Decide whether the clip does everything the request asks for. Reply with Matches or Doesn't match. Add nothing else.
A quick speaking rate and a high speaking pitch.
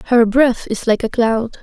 Matches